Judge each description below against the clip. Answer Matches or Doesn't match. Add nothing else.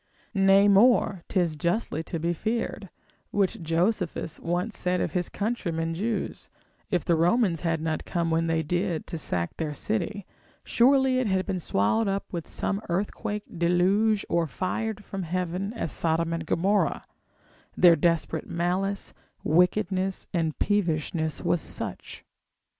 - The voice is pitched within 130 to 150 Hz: Doesn't match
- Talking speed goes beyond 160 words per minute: Doesn't match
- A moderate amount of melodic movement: Matches